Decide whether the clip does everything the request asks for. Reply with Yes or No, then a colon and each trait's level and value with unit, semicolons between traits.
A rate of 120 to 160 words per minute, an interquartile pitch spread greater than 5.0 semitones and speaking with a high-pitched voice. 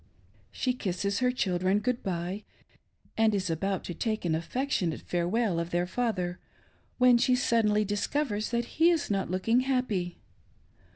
Yes: average, 150 wpm; wide, 5.4 semitones; high, 210 Hz